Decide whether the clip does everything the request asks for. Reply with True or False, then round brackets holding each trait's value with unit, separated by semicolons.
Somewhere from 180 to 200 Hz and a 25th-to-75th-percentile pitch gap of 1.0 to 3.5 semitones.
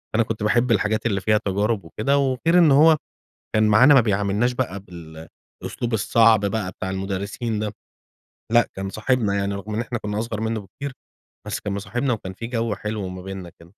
False (110 Hz; 3.2 semitones)